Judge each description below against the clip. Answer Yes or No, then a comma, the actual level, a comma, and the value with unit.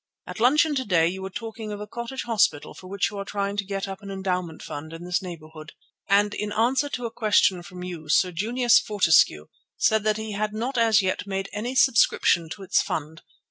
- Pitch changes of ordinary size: Yes, average, 3.6 semitones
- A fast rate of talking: Yes, fast, 220 wpm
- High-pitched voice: Yes, high, 200 Hz